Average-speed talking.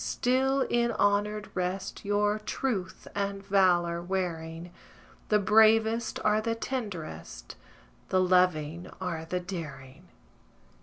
No: slow, 105 wpm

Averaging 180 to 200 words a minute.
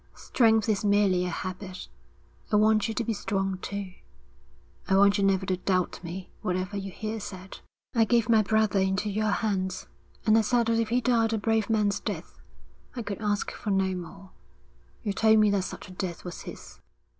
Yes: average, 195 wpm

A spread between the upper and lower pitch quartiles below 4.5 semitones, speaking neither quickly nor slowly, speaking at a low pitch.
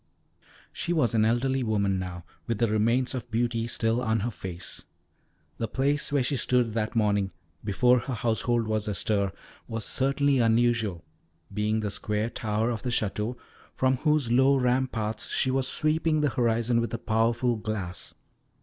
Yes: average, 2.8 semitones; average, 160 wpm; low, 115 Hz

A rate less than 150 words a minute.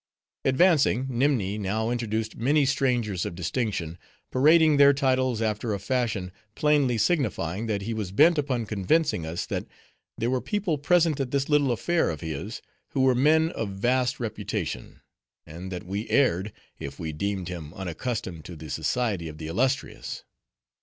No: average, 160 wpm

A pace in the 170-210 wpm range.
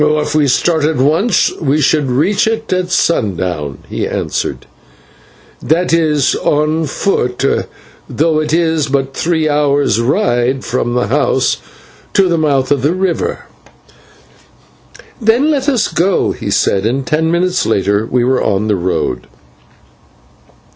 No: average, 140 wpm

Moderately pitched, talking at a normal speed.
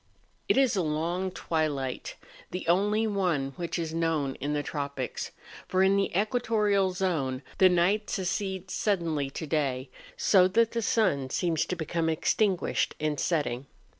Yes: medium, 175 Hz; average, 150 wpm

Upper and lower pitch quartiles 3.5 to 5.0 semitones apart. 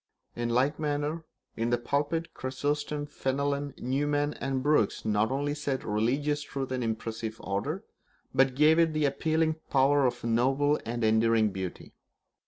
Yes: average, 3.8 semitones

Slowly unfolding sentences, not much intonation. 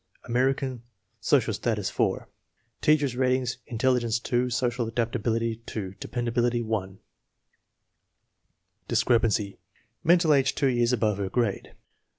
Yes: slow, 110 wpm; narrow, 2.3 semitones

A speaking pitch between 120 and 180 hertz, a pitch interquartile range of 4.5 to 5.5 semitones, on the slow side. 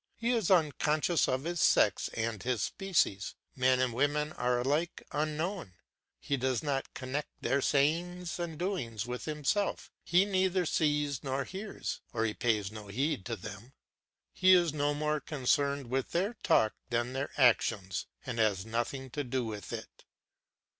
No: medium, 140 Hz; average, 5.2 semitones; average, 160 wpm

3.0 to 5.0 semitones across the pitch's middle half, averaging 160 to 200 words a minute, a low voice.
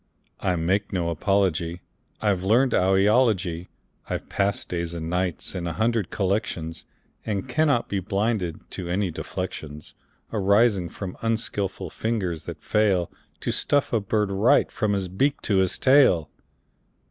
No: average, 3.5 semitones; average, 145 wpm; very low, 95 Hz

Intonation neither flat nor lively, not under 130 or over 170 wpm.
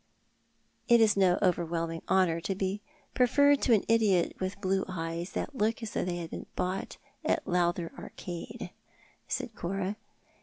Yes: average, 3.4 semitones; average, 165 wpm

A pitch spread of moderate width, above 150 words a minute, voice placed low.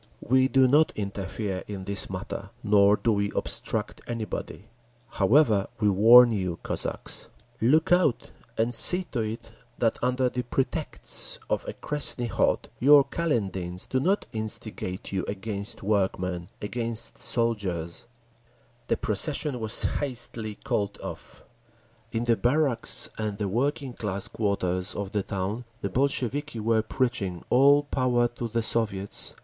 No: average, 4.0 semitones; slow, 135 wpm; low, 110 Hz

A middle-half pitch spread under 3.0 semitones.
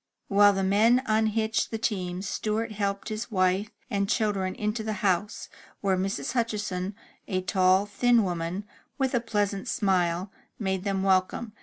Yes: narrow, 2.5 semitones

